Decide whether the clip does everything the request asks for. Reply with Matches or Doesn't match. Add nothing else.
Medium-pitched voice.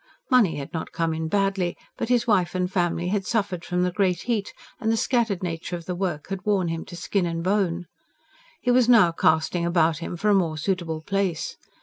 Matches